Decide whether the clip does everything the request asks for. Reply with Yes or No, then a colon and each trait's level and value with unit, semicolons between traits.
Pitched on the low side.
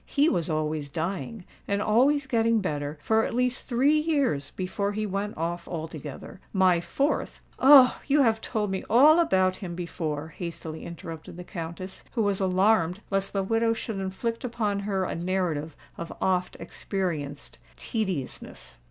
No: high, 190 Hz